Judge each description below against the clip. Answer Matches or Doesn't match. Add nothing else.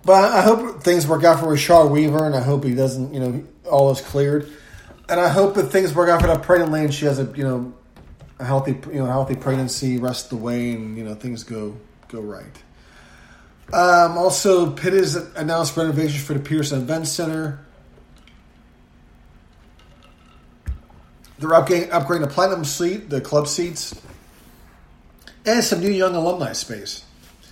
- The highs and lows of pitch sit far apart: Matches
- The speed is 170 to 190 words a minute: Matches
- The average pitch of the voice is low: Doesn't match